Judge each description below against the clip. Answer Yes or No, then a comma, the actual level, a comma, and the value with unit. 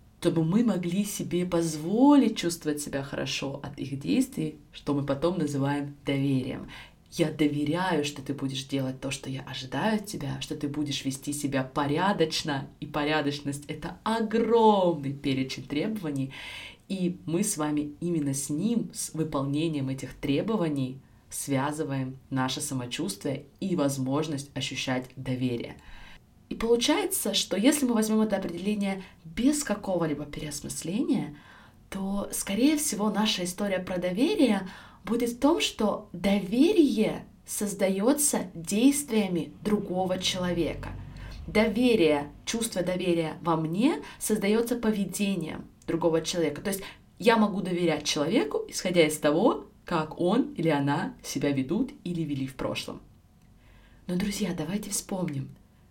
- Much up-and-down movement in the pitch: Yes, wide, 6.3 semitones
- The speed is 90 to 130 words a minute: Yes, average, 125 wpm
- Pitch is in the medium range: Yes, medium, 165 Hz